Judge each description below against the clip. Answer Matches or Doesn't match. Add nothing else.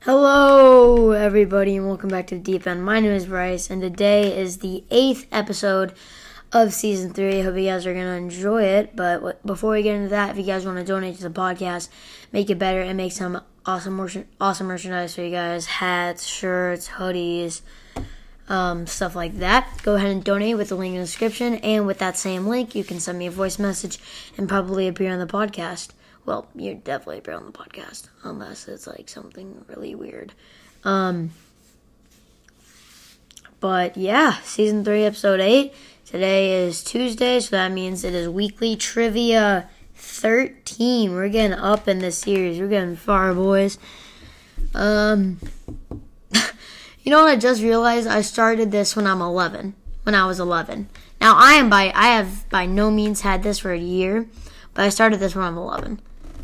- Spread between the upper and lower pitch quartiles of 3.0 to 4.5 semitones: Doesn't match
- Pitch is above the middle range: Matches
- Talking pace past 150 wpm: Matches